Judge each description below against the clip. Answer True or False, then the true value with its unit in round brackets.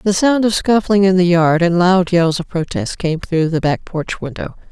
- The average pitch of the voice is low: False (180 Hz)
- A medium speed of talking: False (230 wpm)